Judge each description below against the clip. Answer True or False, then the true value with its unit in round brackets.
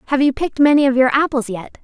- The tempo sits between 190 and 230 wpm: False (260 wpm)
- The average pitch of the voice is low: False (270 Hz)